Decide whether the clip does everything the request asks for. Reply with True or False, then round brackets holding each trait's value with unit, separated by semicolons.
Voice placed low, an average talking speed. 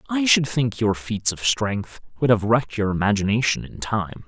True (115 Hz; 195 wpm)